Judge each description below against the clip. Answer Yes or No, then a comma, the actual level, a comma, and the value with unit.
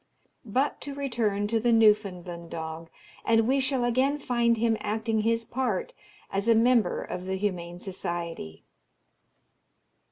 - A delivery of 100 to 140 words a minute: Yes, slow, 135 wpm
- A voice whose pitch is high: Yes, high, 220 Hz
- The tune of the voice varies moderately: Yes, average, 4.6 semitones